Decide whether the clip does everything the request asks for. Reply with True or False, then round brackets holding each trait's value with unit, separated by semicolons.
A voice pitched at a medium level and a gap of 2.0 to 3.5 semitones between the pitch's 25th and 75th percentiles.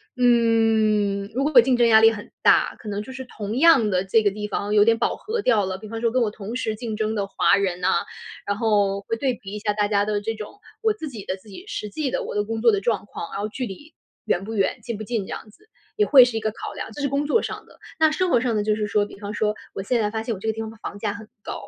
False (220 Hz; 2.8 semitones)